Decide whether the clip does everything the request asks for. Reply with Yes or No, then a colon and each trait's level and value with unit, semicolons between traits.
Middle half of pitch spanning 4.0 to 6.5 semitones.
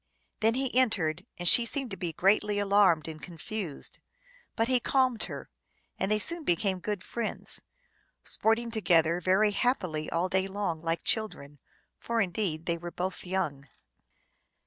Yes: average, 4.7 semitones